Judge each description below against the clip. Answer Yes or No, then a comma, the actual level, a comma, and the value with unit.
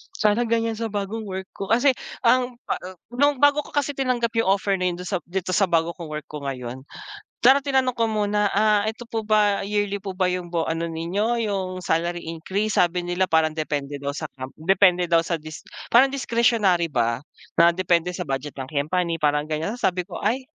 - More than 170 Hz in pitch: Yes, medium, 185 Hz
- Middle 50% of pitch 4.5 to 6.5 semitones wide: Yes, average, 5.1 semitones